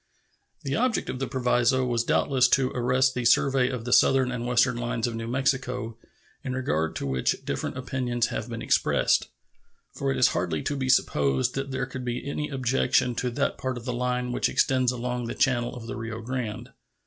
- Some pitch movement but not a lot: No, narrow, 1.7 semitones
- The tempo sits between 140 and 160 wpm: No, average, 200 wpm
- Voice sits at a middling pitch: No, low, 125 Hz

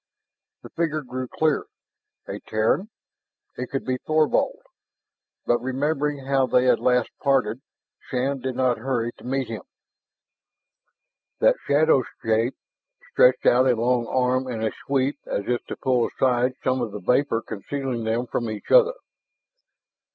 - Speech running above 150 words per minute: No, average, 145 wpm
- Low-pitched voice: Yes, low, 130 Hz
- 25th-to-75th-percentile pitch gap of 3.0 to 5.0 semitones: No, narrow, 2.4 semitones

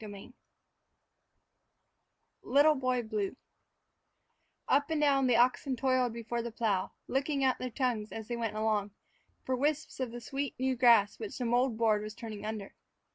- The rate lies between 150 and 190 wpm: Yes, average, 160 wpm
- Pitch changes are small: No, average, 3.2 semitones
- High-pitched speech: Yes, high, 240 Hz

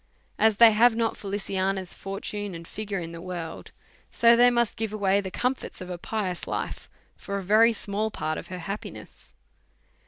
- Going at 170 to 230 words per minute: Yes, average, 180 wpm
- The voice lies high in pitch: Yes, high, 200 Hz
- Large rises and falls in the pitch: No, average, 3.1 semitones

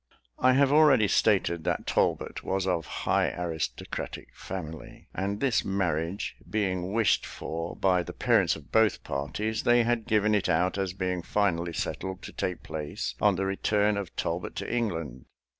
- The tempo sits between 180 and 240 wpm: No, average, 160 wpm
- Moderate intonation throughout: Yes, average, 3.7 semitones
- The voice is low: Yes, very low, 95 Hz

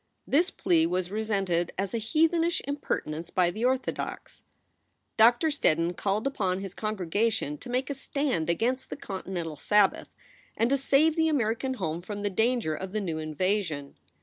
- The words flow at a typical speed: Yes, average, 160 wpm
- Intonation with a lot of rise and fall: Yes, wide, 6.7 semitones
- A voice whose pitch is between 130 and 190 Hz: No, high, 210 Hz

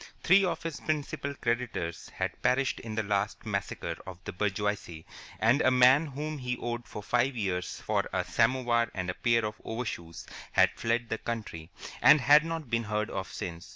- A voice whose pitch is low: Yes, low, 115 Hz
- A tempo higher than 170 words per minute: Yes, average, 185 wpm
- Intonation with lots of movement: No, average, 4.0 semitones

